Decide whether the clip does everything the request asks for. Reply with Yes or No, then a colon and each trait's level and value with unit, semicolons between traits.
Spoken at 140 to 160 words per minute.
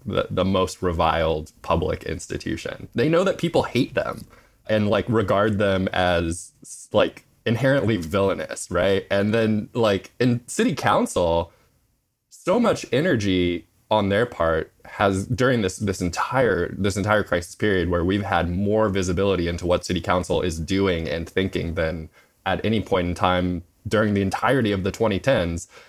Yes: average, 155 wpm